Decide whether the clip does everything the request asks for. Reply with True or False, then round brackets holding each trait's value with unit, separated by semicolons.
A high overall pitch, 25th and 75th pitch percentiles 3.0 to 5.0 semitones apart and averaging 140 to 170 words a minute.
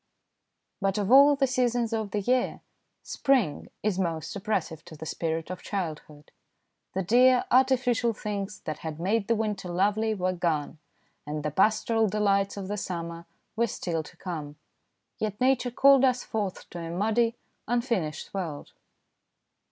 False (200 Hz; 5.5 semitones; 155 wpm)